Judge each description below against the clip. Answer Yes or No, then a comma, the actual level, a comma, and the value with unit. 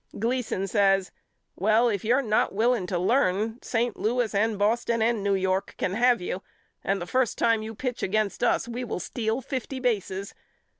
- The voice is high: Yes, high, 220 Hz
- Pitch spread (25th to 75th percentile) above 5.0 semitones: No, average, 3.5 semitones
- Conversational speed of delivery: Yes, average, 180 wpm